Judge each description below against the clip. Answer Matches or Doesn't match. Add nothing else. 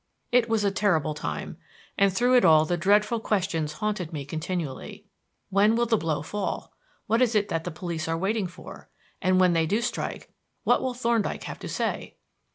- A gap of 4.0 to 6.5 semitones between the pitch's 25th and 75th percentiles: Matches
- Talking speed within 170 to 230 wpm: Matches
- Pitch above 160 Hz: Matches